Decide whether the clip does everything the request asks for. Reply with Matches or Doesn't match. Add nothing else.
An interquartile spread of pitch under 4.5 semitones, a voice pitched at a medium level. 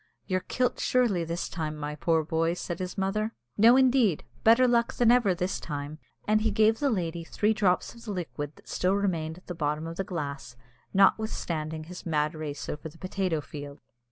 Doesn't match